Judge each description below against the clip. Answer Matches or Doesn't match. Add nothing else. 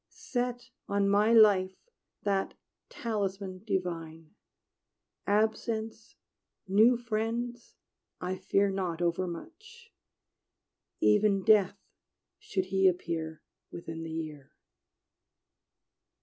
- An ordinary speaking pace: Doesn't match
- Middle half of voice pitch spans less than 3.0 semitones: Doesn't match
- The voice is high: Matches